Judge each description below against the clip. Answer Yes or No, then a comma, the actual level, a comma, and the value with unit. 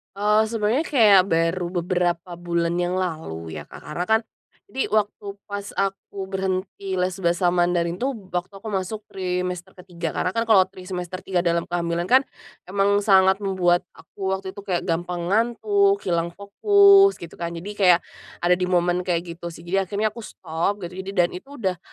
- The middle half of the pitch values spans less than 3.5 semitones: Yes, narrow, 2.5 semitones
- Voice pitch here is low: No, medium, 185 Hz